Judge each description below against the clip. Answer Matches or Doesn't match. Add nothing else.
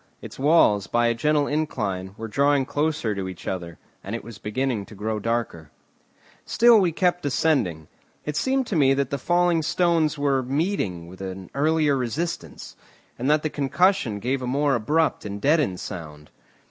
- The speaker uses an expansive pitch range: Matches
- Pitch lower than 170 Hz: Matches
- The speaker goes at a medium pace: Matches